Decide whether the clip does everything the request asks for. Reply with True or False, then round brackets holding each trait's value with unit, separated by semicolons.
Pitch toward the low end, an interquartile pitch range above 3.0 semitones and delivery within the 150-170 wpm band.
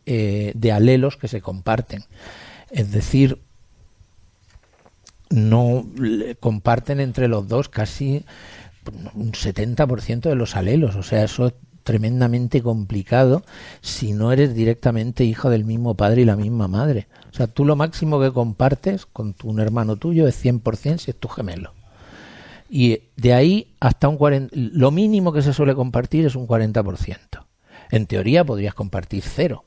True (115 Hz; 4.0 semitones; 155 wpm)